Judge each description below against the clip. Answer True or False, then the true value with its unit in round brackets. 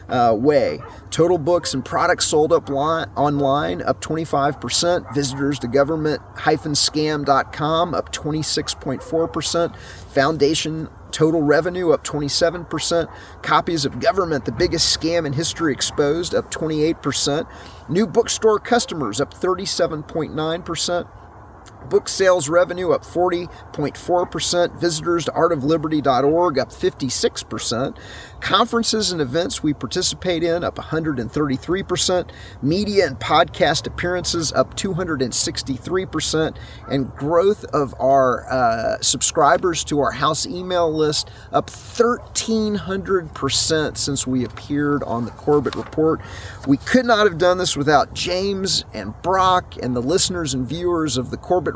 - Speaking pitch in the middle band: True (155 Hz)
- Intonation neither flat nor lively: True (4.5 semitones)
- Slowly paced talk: True (115 wpm)